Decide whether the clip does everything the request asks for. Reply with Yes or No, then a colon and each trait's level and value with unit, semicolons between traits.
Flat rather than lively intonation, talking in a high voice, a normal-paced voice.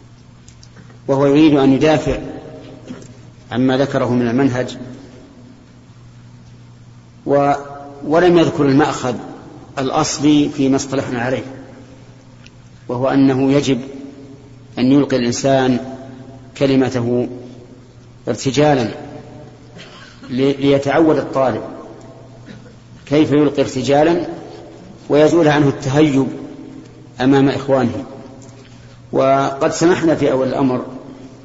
No: narrow, 2.0 semitones; low, 130 Hz; average, 75 wpm